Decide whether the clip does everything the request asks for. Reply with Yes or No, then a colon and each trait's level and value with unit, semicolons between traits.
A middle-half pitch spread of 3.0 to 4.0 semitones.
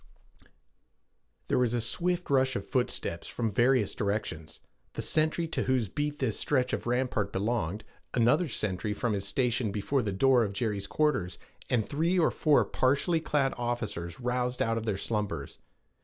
No: average, 4.5 semitones